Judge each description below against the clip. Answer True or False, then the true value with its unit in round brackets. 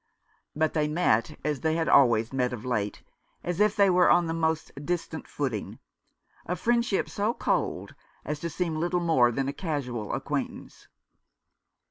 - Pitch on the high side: False (160 Hz)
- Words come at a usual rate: True (170 wpm)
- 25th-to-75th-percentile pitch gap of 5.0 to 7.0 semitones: True (5.5 semitones)